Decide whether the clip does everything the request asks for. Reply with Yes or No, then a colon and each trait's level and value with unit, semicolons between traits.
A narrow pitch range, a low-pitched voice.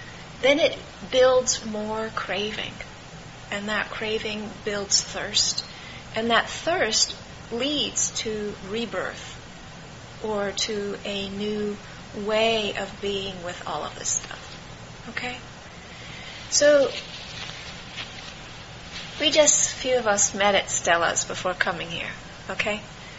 No: narrow, 2.1 semitones; high, 215 Hz